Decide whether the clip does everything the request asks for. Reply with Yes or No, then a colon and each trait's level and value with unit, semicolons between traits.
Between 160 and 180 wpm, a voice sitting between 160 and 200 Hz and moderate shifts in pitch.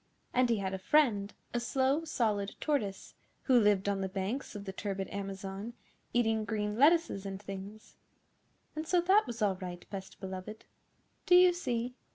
No: average, 170 wpm; high, 210 Hz; average, 4.6 semitones